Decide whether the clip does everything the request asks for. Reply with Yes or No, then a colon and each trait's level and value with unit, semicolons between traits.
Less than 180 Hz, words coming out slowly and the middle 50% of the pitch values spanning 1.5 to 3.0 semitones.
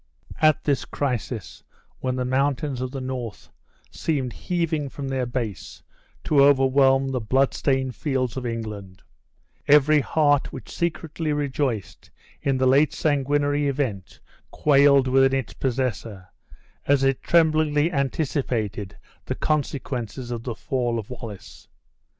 Yes: low, 135 Hz; slow, 125 wpm; average, 2.7 semitones